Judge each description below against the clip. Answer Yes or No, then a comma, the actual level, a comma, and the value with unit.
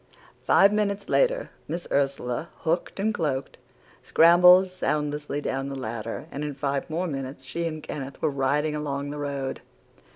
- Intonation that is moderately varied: Yes, average, 3.7 semitones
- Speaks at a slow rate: No, average, 155 wpm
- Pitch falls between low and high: Yes, medium, 150 Hz